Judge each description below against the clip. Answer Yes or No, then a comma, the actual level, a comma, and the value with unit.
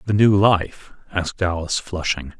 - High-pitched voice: No, very low, 90 Hz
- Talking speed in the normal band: Yes, average, 150 wpm